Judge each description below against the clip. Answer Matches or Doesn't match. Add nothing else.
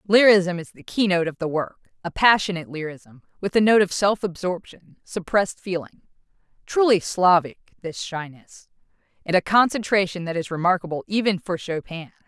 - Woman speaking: Matches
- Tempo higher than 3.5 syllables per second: Matches